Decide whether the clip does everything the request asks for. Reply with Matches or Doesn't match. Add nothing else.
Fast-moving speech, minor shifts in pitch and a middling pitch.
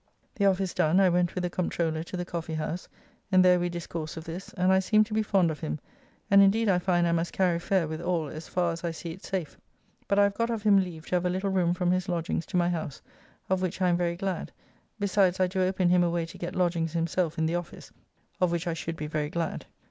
Matches